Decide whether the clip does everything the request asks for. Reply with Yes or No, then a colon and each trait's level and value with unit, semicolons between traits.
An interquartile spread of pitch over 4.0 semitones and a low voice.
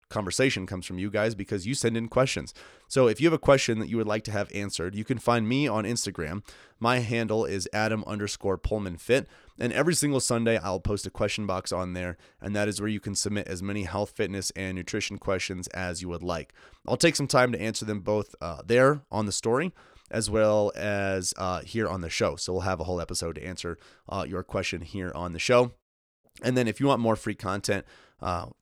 No: average, 3.5 semitones; low, 105 Hz